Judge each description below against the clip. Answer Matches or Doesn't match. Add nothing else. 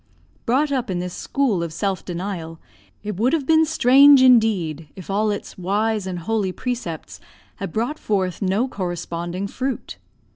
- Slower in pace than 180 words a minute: Matches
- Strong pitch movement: Matches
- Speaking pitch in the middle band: Doesn't match